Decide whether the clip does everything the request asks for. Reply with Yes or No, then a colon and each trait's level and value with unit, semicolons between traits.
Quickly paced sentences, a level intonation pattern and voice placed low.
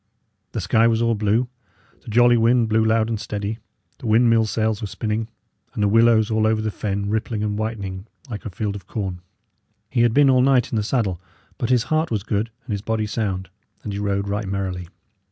Yes: fast, 210 wpm; narrow, 2.1 semitones; low, 110 Hz